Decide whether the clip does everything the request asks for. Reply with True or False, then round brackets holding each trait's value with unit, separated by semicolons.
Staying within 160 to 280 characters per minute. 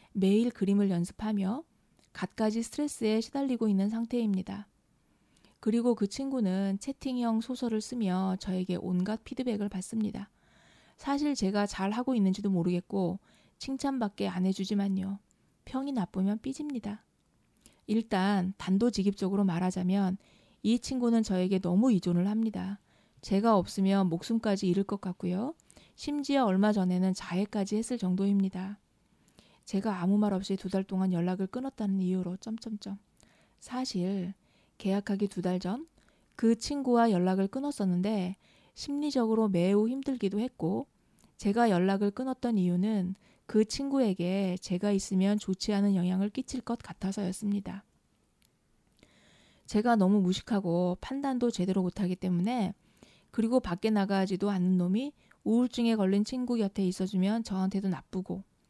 False (310 characters per minute)